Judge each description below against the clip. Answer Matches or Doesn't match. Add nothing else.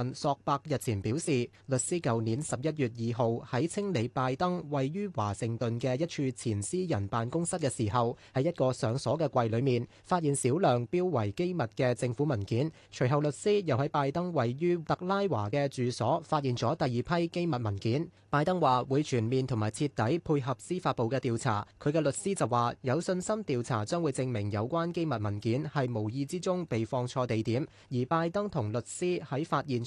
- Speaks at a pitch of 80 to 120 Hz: Doesn't match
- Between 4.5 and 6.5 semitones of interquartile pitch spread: Matches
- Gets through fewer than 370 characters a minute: Matches